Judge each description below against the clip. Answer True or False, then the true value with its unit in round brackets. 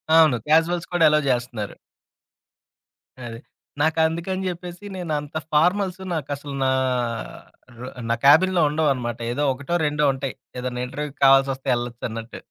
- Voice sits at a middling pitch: True (150 Hz)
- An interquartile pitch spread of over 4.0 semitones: True (4.6 semitones)